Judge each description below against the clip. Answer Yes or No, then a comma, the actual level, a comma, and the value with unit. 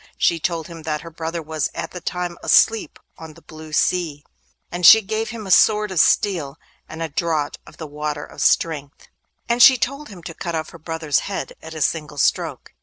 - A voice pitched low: No, medium, 165 Hz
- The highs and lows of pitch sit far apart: No, average, 2.9 semitones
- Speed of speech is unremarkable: No, fast, 210 wpm